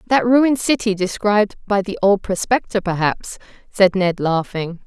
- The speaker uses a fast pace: No, average, 150 wpm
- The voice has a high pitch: Yes, high, 200 Hz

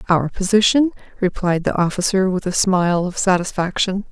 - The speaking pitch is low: No, high, 190 Hz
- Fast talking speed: No, average, 145 wpm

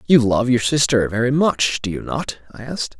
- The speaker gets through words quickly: Yes, fast, 220 wpm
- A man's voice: Yes, male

